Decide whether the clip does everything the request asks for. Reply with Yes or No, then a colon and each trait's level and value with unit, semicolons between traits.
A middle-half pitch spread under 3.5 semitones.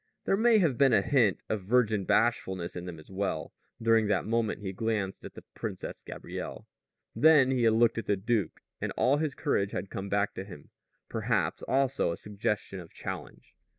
No: average, 4.3 semitones